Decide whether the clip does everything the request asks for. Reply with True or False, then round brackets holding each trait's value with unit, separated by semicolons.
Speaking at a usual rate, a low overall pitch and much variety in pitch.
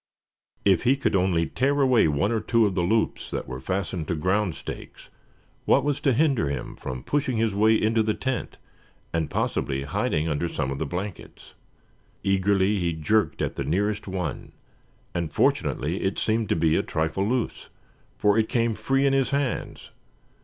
True (180 wpm; 100 Hz; 5.7 semitones)